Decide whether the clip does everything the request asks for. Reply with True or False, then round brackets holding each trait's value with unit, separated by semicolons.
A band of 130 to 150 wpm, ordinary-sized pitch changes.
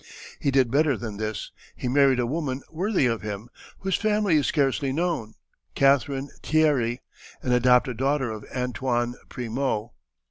True (145 wpm; 3.3 semitones)